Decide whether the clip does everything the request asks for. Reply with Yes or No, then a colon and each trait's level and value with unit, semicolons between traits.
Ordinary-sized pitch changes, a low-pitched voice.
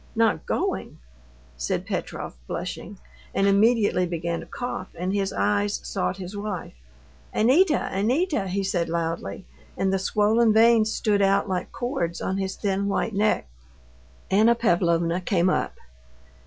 No: average, 3.2 semitones; high, 200 Hz